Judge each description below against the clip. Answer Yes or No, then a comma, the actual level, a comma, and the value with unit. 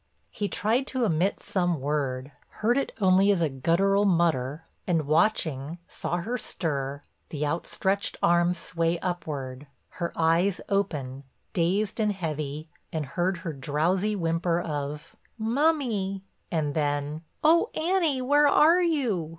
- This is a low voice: No, medium, 175 Hz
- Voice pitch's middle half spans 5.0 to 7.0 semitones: Yes, average, 5.3 semitones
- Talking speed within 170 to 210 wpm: No, slow, 135 wpm